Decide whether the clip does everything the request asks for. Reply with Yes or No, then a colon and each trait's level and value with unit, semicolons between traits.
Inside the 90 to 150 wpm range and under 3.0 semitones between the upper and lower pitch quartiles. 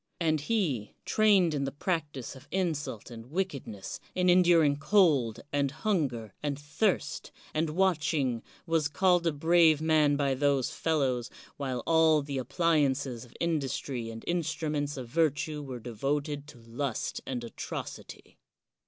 No: average, 145 wpm; average, 3.7 semitones